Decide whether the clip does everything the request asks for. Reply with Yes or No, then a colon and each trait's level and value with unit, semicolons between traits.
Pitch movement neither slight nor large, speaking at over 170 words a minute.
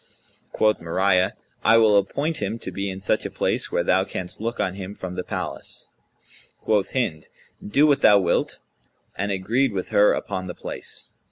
Yes: average, 3.1 semitones; average, 180 wpm